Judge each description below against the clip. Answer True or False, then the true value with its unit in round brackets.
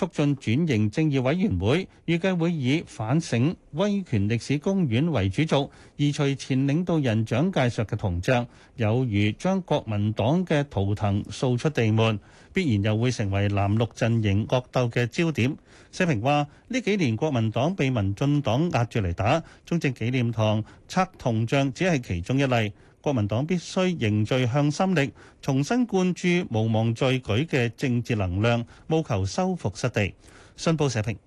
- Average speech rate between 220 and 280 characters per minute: True (245 characters per minute)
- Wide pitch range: True (6.3 semitones)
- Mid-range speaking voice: False (130 Hz)